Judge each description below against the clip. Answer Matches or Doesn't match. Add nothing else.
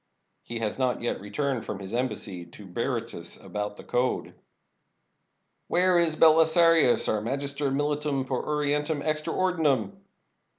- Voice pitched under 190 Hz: Matches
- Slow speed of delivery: Doesn't match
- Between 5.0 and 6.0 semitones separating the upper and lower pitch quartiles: Matches